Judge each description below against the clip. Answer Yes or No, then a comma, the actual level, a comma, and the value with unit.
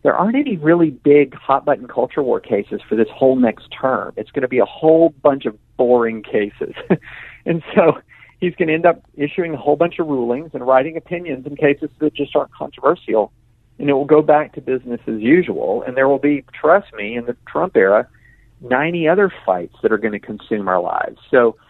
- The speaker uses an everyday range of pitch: Yes, average, 4.5 semitones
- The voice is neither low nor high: Yes, medium, 145 Hz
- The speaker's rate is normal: No, fast, 215 wpm